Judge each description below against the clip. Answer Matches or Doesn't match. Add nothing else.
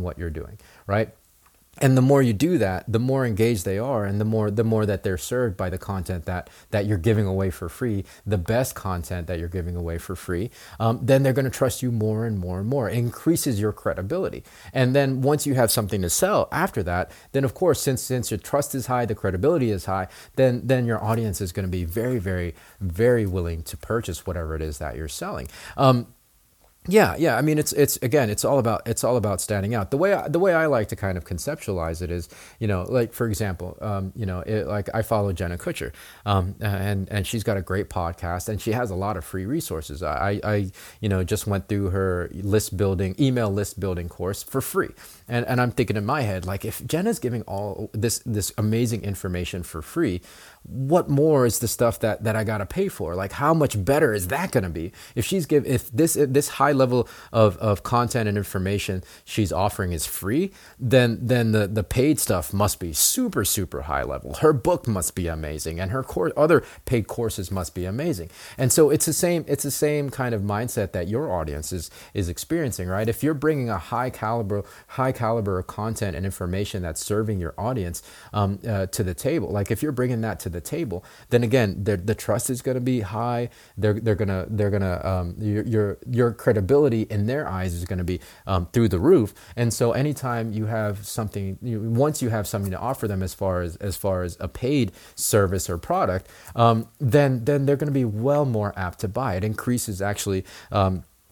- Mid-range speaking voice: Doesn't match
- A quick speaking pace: Matches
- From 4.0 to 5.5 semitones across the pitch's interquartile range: Matches